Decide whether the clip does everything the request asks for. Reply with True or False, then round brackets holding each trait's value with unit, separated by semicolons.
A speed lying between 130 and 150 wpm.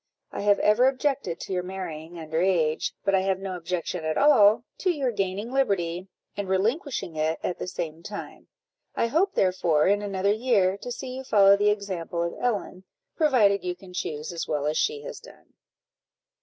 False (185 wpm)